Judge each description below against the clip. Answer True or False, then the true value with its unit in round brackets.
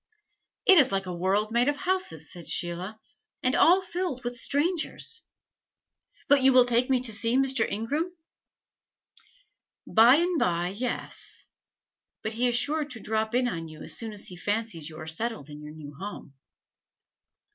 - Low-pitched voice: False (230 Hz)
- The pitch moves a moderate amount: False (6.7 semitones)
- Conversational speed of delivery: True (170 wpm)